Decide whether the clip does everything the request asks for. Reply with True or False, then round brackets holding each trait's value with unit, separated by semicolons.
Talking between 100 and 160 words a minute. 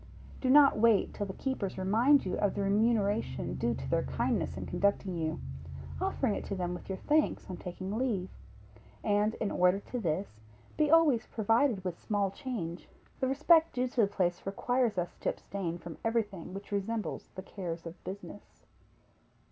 False (175 wpm)